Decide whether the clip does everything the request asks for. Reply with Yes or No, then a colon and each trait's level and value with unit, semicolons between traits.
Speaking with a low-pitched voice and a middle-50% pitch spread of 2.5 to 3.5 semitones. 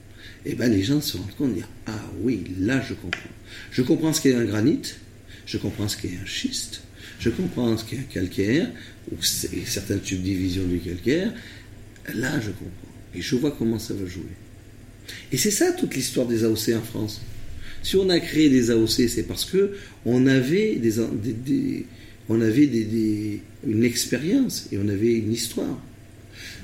Yes: low, 110 Hz; average, 3.2 semitones